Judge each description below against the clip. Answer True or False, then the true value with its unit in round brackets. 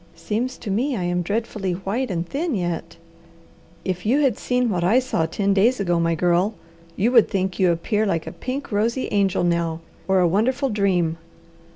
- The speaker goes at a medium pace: True (190 wpm)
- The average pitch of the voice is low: False (195 Hz)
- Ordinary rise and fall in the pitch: True (5.0 semitones)